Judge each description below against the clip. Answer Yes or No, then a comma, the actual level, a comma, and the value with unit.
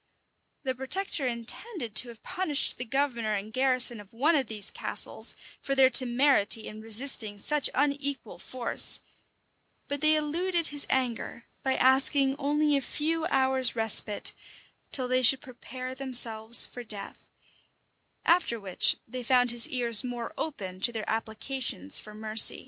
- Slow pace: No, average, 145 wpm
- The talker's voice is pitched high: Yes, very high, 255 Hz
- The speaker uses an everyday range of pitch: Yes, average, 3.8 semitones